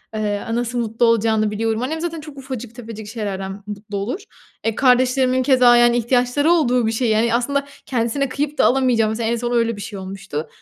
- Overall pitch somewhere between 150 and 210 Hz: No, high, 235 Hz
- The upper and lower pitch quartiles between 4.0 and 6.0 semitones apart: No, average, 2.9 semitones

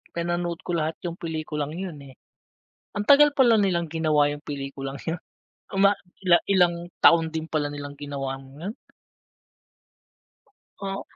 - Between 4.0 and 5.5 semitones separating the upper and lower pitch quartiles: No, average, 3.5 semitones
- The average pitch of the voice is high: No, medium, 165 Hz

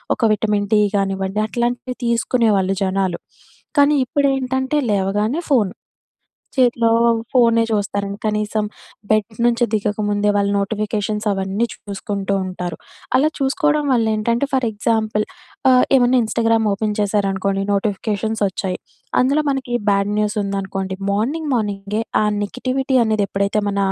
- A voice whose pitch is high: Yes, high, 215 Hz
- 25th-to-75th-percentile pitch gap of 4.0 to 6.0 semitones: No, average, 3.2 semitones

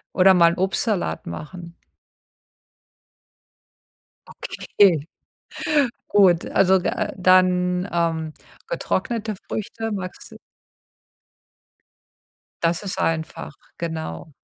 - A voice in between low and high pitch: Yes, medium, 180 Hz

